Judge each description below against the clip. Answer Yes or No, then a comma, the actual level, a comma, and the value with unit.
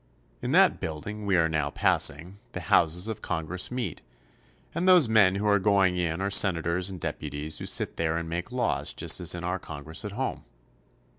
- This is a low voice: Yes, very low, 90 Hz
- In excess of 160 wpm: Yes, average, 200 wpm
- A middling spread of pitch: Yes, average, 4.0 semitones